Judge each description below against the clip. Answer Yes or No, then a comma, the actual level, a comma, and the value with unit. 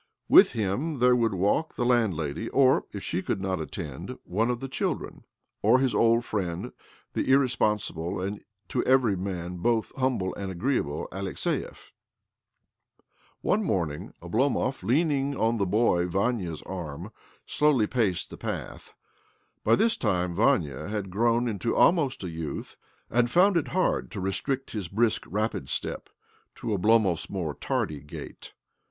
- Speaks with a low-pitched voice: Yes, low, 105 Hz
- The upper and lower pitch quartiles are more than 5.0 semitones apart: Yes, wide, 5.6 semitones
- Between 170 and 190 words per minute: No, average, 145 wpm